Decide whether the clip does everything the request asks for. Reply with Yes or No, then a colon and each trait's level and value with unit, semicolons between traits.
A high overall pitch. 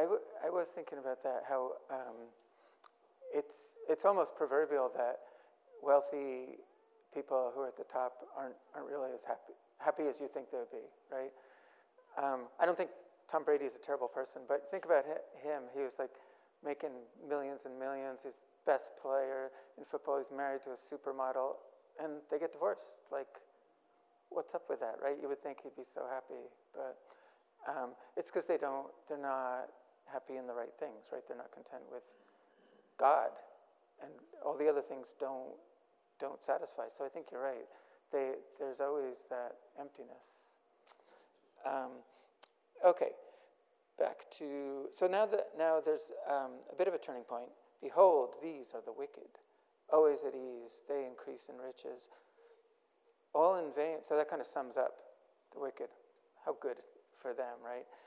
No: medium, 140 Hz